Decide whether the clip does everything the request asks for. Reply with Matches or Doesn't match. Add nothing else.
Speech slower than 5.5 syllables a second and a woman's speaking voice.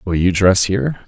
Doesn't match